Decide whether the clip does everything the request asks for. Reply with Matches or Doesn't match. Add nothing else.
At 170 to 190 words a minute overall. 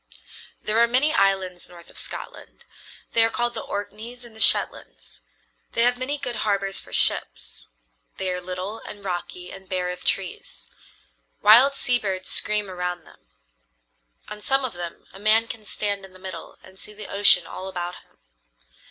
Matches